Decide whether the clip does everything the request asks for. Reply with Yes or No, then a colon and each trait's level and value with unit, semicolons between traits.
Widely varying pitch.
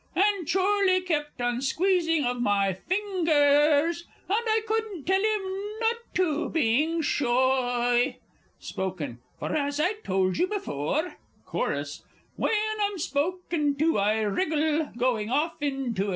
Yes: wide, 7.0 semitones